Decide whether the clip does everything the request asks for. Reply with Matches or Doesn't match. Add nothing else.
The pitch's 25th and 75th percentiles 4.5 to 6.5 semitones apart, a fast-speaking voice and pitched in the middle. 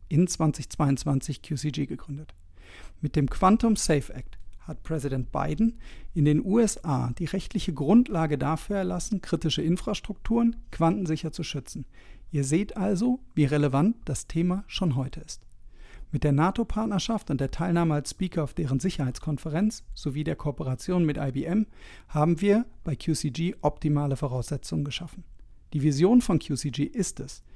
Doesn't match